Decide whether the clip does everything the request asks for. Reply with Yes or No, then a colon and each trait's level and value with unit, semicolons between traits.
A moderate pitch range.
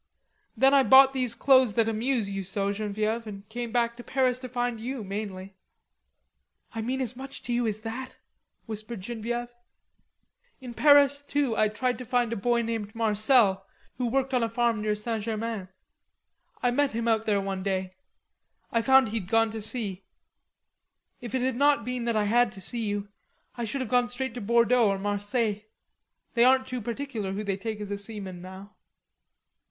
Yes: average, 3.1 semitones